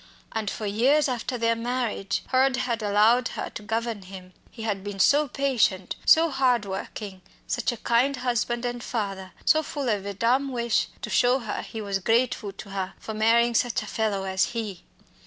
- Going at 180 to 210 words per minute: Yes, average, 190 wpm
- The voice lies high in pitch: Yes, high, 230 Hz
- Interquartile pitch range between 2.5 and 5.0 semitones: Yes, average, 3.5 semitones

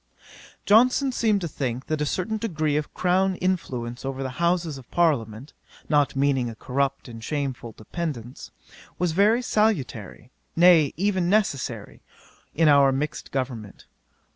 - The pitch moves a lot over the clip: Yes, wide, 5.8 semitones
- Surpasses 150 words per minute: No, average, 140 wpm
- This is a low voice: No, medium, 150 Hz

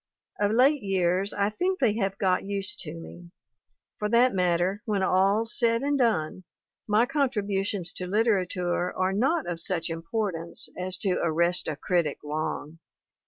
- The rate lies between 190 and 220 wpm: No, average, 155 wpm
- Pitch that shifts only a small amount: No, average, 3.9 semitones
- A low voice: No, high, 195 Hz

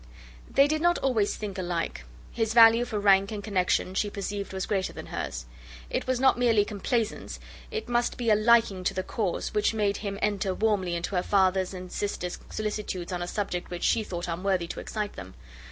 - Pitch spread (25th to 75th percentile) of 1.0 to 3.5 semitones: Yes, average, 3.2 semitones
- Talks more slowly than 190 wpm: No, average, 200 wpm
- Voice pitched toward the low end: No, high, 205 Hz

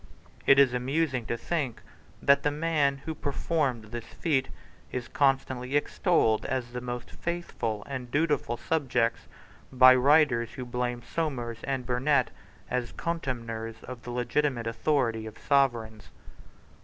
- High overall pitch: No, low, 130 Hz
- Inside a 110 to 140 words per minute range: Yes, slow, 135 wpm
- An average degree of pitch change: Yes, average, 3.2 semitones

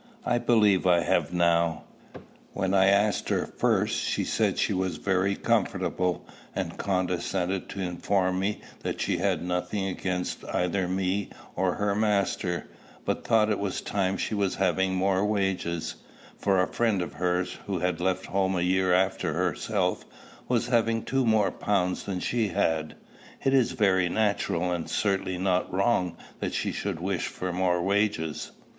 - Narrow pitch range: Yes, narrow, 2.0 semitones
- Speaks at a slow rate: No, average, 160 wpm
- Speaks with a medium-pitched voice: No, very low, 95 Hz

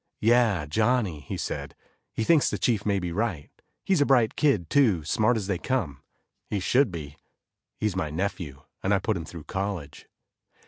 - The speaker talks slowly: No, average, 180 wpm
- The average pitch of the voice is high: No, low, 100 Hz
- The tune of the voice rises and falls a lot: Yes, wide, 5.9 semitones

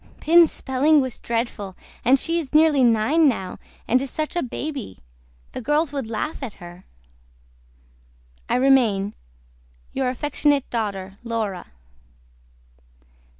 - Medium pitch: No, very high, 255 Hz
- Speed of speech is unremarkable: No, slow, 120 wpm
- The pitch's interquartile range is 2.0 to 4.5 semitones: No, average, 5.2 semitones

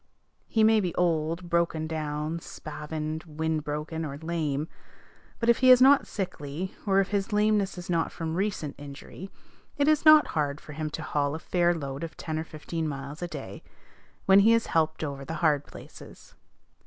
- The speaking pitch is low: No, medium, 160 Hz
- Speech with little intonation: No, average, 4.0 semitones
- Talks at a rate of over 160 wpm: Yes, average, 180 wpm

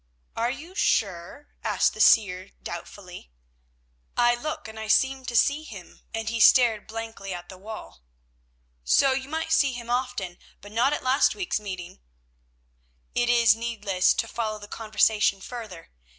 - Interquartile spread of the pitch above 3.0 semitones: Yes, average, 4.0 semitones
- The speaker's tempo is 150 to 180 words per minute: Yes, average, 160 wpm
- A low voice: No, high, 225 Hz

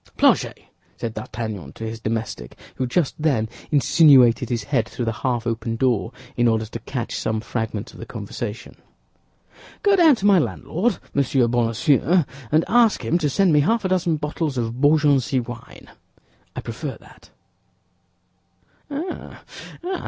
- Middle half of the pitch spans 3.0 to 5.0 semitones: No, wide, 5.5 semitones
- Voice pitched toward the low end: Yes, low, 125 Hz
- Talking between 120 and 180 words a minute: Yes, average, 145 wpm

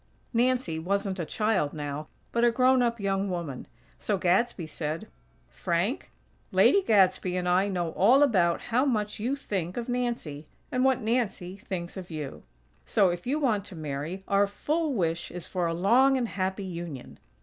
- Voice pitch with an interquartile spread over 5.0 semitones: Yes, wide, 5.5 semitones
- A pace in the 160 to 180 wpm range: Yes, average, 170 wpm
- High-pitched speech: Yes, high, 195 Hz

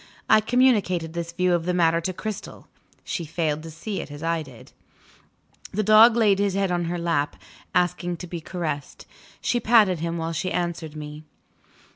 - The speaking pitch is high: No, medium, 175 Hz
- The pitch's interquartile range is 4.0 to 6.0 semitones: No, average, 3.1 semitones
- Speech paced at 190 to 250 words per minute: No, average, 180 wpm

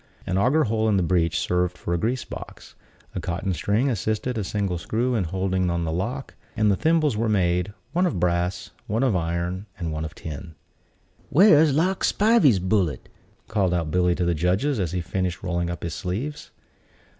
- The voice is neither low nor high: No, very low, 95 Hz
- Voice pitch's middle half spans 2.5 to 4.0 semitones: No, average, 5.0 semitones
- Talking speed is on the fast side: No, average, 190 wpm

